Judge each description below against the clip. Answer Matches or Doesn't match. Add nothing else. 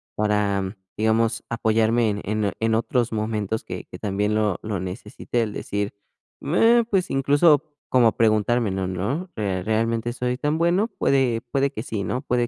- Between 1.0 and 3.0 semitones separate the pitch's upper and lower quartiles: Doesn't match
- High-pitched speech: Doesn't match